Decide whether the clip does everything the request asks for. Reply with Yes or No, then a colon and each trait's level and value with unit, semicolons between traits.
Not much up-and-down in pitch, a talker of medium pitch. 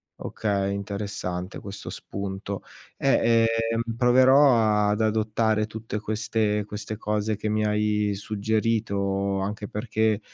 No: narrow, 1.6 semitones; low, 105 Hz